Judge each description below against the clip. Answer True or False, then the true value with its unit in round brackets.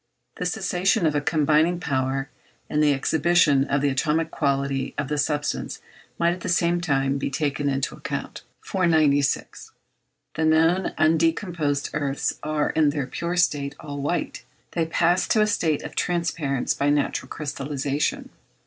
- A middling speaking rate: True (155 wpm)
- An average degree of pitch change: True (3.2 semitones)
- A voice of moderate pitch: True (150 Hz)